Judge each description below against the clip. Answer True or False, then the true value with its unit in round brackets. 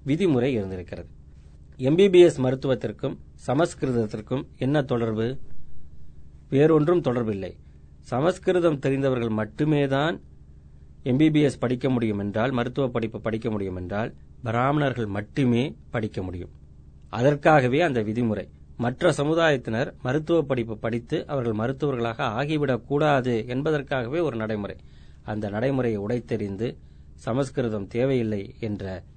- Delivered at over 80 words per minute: True (95 wpm)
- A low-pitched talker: True (120 Hz)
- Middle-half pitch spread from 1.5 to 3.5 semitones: False (5.5 semitones)